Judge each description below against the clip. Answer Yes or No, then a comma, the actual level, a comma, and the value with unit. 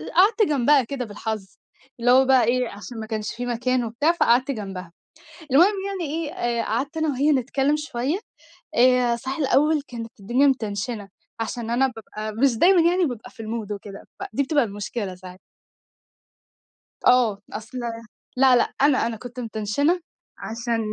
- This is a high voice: Yes, high, 245 Hz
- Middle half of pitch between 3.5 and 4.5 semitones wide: Yes, average, 4.0 semitones